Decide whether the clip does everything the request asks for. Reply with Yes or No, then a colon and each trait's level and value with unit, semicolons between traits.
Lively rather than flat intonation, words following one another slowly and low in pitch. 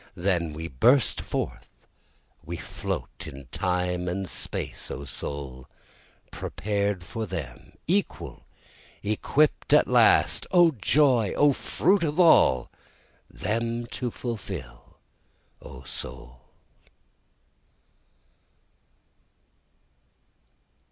Yes: wide, 8.3 semitones; slow, 85 wpm; low, 100 Hz